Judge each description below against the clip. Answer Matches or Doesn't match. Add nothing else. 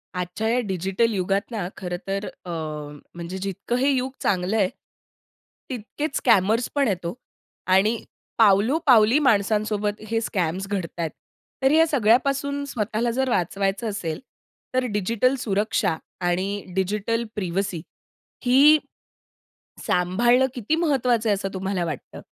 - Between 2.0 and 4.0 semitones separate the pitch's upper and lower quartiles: Doesn't match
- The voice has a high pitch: Matches